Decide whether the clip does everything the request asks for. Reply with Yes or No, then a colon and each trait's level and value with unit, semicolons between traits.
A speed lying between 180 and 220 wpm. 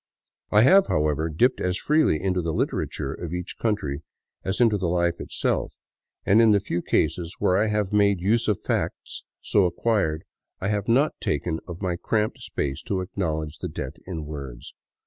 Yes: average, 185 wpm